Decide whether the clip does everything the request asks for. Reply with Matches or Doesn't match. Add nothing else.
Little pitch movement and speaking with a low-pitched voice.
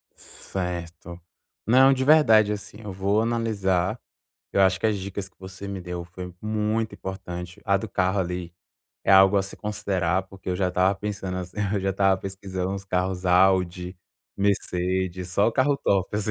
Matches